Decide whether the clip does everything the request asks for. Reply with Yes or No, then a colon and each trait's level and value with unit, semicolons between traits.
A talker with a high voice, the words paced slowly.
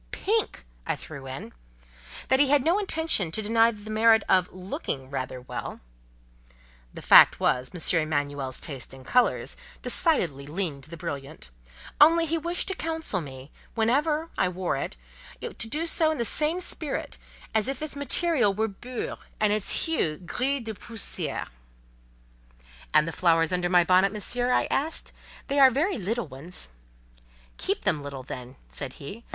No: high, 205 Hz; average, 165 wpm